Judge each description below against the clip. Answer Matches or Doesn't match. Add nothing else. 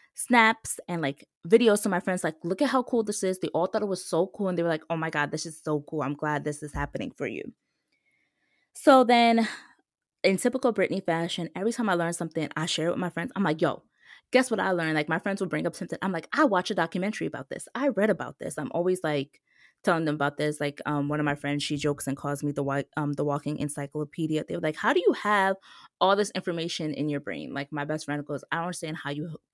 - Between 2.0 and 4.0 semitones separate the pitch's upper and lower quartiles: Doesn't match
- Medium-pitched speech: Matches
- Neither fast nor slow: Doesn't match